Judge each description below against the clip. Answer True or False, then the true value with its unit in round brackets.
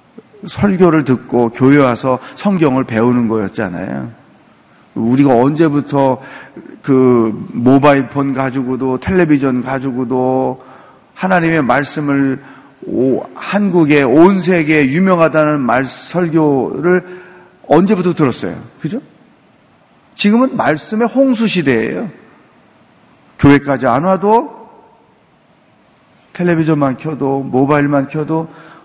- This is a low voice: False (145 Hz)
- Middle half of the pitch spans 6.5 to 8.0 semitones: False (5.1 semitones)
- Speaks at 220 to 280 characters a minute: True (230 characters per minute)